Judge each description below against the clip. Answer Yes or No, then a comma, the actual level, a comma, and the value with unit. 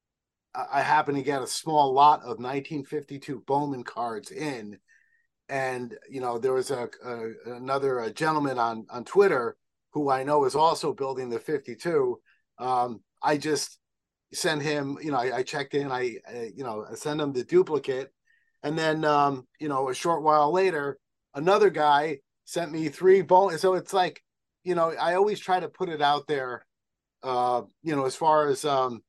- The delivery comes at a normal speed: Yes, average, 180 wpm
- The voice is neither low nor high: Yes, medium, 145 Hz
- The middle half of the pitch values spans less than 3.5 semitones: No, average, 4.4 semitones